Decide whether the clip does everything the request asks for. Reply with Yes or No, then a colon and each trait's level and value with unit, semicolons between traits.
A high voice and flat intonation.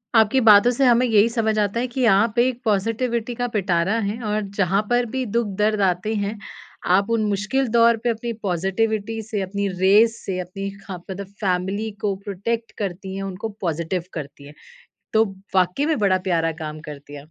No: high, 205 Hz; average, 3.6 semitones